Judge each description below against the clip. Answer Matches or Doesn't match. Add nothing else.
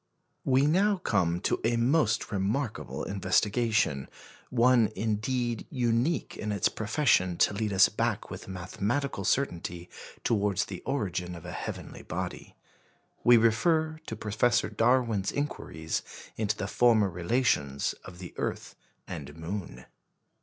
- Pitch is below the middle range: Matches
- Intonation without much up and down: Doesn't match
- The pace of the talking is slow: Matches